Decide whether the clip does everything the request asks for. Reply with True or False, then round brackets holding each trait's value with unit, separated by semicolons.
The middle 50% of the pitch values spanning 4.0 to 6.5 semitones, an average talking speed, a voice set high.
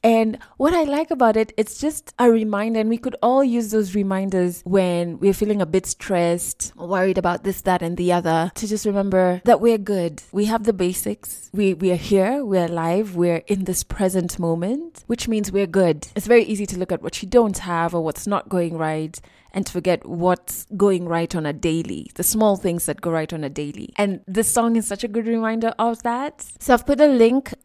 False (4.5 semitones; 225 wpm; 195 Hz)